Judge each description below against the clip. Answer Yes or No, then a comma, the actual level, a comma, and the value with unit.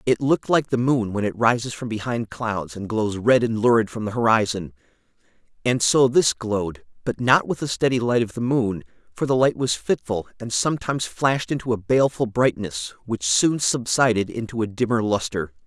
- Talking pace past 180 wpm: Yes, average, 195 wpm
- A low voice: Yes, low, 120 Hz